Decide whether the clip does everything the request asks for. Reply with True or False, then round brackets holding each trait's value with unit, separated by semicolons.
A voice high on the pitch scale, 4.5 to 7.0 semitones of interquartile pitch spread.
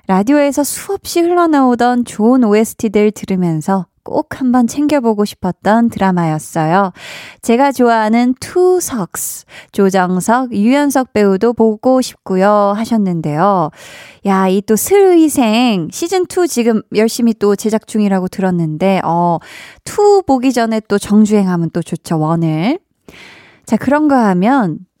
True (220 Hz; 5.1 semitones)